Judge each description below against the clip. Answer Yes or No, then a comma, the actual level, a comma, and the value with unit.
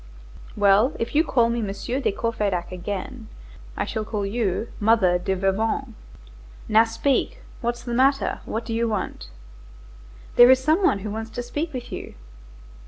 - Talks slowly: No, average, 165 wpm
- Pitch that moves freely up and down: No, average, 3.4 semitones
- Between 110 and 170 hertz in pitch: No, high, 225 Hz